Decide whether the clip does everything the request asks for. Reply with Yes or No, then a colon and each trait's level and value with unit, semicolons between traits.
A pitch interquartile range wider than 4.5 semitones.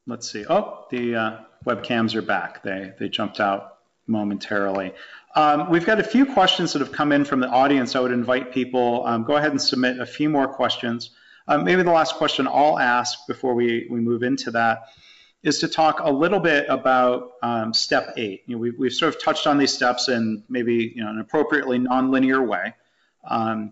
No: average, 3.4 semitones